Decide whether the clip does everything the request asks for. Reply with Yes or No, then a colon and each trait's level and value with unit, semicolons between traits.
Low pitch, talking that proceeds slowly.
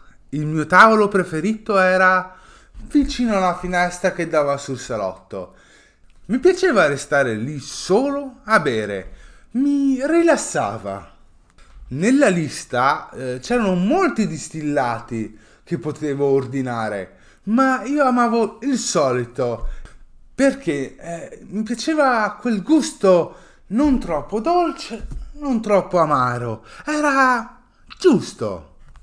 No: high, 190 Hz; slow, 100 wpm